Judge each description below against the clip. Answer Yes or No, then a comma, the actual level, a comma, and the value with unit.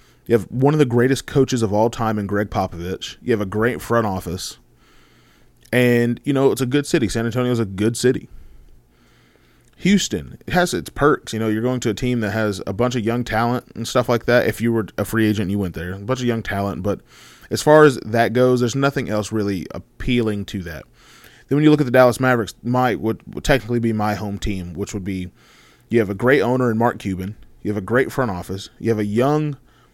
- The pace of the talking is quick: Yes, fast, 240 wpm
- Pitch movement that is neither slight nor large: Yes, average, 3.7 semitones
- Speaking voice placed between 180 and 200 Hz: No, low, 115 Hz